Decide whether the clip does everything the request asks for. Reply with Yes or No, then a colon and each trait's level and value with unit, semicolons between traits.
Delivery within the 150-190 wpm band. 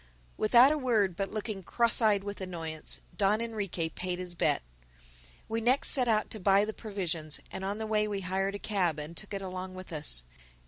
No: average, 200 wpm